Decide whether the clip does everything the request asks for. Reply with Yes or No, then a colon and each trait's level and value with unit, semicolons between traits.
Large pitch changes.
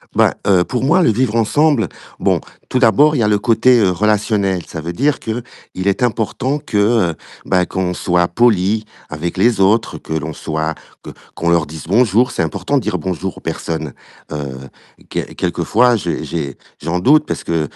Yes: wide, 6.0 semitones